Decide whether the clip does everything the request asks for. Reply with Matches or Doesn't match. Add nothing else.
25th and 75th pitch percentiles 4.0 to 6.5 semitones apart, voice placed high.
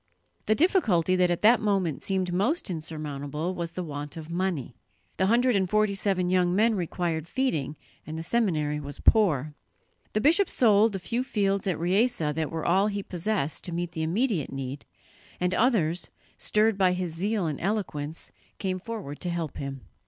Doesn't match